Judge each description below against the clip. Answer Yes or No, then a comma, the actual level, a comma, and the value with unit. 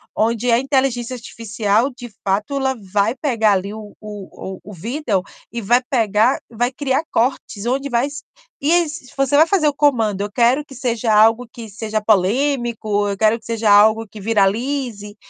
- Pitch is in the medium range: No, high, 230 Hz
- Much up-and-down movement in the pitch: No, average, 4.0 semitones